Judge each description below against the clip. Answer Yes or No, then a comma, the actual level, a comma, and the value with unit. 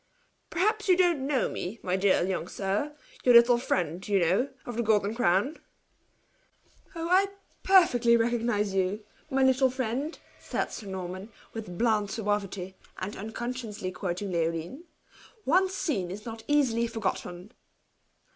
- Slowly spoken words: No, average, 145 wpm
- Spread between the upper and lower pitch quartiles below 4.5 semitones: No, wide, 5.5 semitones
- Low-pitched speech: No, high, 225 Hz